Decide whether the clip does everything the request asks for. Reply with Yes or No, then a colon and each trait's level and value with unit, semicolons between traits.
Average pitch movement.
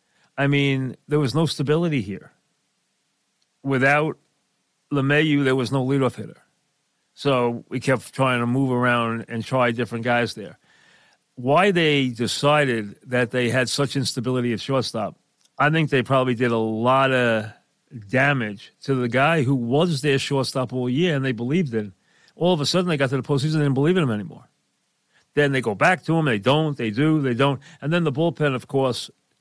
Yes: average, 3.0 semitones